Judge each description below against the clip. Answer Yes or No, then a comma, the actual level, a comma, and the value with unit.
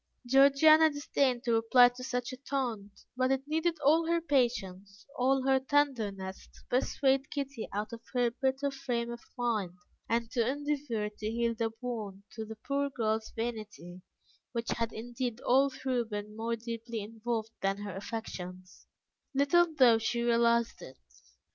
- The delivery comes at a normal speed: Yes, average, 155 wpm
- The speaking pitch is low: No, high, 235 Hz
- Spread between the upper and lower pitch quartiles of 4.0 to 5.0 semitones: No, average, 3.4 semitones